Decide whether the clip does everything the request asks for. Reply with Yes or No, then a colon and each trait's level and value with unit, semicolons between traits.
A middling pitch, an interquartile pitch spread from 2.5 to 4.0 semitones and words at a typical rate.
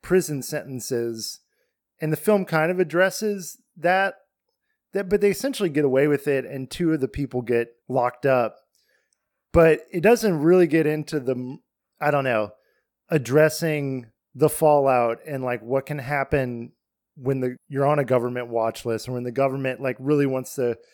No: medium, 145 Hz; average, 4.6 semitones; average, 170 wpm